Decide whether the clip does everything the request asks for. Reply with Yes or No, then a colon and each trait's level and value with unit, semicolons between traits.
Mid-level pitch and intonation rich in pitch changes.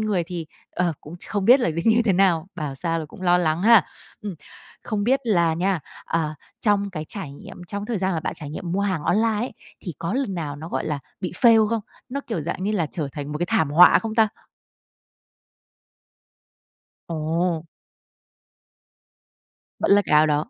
No: medium, 180 Hz; average, 4.5 semitones